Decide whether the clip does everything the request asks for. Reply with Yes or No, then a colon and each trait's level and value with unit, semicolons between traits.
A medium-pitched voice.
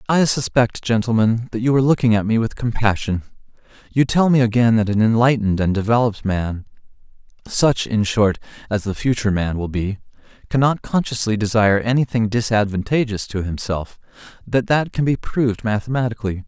No: low, 115 Hz